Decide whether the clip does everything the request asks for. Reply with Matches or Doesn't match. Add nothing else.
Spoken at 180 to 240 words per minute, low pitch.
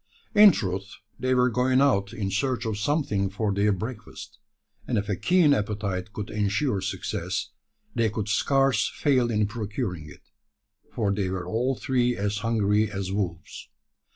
Doesn't match